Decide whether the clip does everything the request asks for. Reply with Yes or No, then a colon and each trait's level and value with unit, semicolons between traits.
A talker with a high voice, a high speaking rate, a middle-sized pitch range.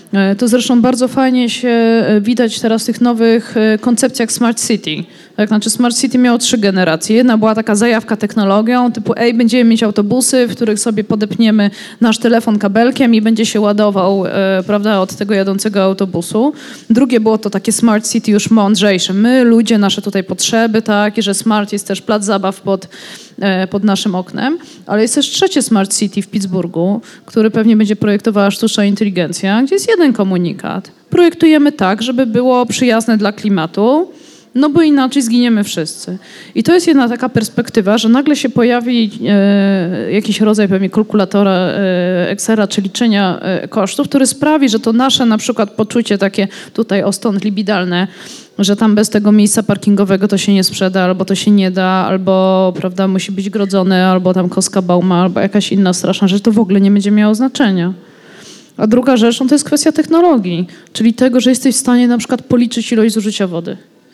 Yes: high, 215 Hz; fast, 180 wpm; average, 3.3 semitones